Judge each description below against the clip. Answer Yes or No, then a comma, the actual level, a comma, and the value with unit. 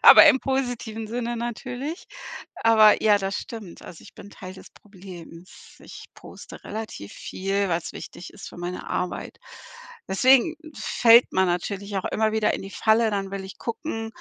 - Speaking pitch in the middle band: No, high, 210 Hz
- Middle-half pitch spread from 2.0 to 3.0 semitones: No, average, 3.4 semitones